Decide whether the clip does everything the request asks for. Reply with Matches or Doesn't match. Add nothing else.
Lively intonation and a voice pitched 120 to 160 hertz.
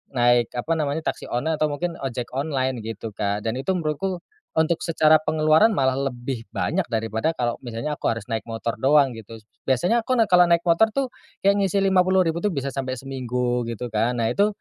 Matches